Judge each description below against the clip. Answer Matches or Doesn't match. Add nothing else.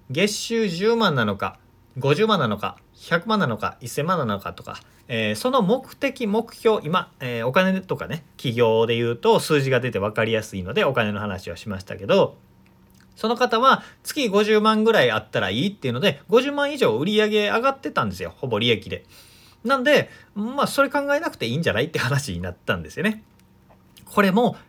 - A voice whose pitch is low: Doesn't match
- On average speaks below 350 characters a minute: Matches